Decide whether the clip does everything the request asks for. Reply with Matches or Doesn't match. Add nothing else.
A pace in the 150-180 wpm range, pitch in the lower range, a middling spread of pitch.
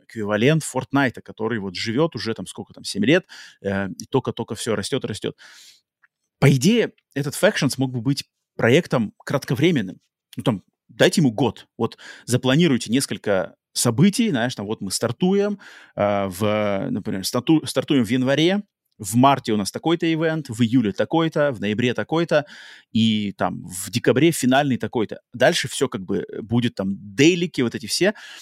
Doesn't match